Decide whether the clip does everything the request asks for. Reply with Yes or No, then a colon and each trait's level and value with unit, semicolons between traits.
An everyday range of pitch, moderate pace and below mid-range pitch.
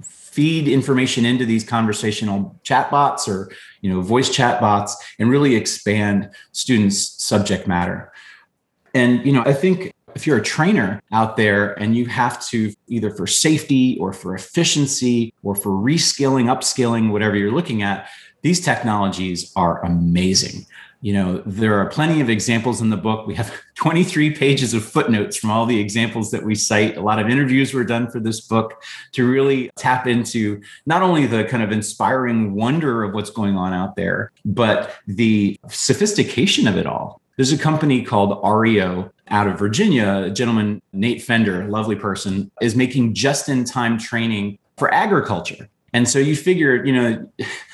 Yes: average, 4.0 semitones; average, 170 wpm; low, 115 Hz